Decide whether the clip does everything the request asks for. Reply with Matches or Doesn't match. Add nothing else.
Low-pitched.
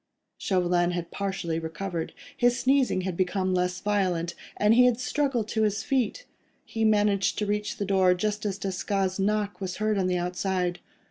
Doesn't match